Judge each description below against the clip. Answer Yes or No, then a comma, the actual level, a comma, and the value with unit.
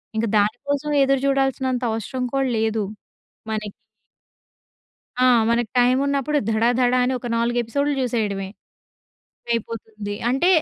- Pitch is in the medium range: No, high, 245 Hz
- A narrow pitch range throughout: No, average, 3.5 semitones